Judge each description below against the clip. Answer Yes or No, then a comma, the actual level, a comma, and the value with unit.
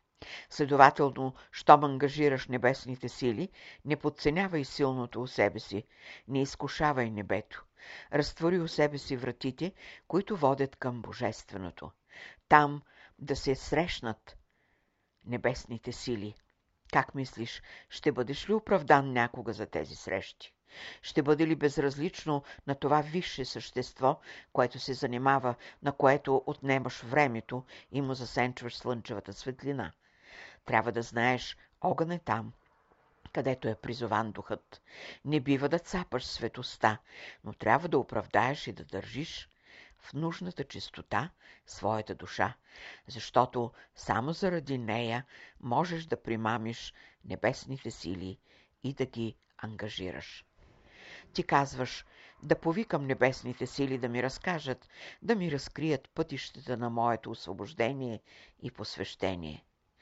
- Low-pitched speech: Yes, low, 130 Hz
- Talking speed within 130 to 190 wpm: No, slow, 115 wpm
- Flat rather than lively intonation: No, average, 4.0 semitones